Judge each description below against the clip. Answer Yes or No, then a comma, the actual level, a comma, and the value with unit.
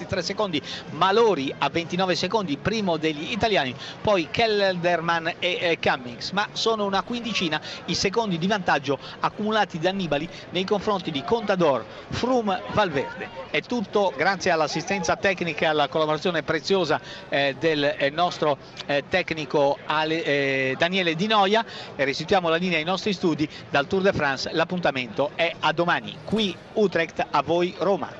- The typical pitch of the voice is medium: Yes, medium, 175 Hz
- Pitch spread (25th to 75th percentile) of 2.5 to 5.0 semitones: Yes, average, 4.2 semitones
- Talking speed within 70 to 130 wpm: No, average, 150 wpm